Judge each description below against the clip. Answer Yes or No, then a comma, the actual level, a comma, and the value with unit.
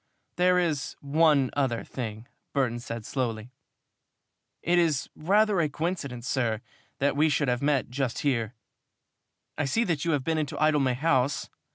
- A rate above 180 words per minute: No, average, 155 wpm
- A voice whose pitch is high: No, medium, 140 Hz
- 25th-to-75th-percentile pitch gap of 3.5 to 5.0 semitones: Yes, average, 4.2 semitones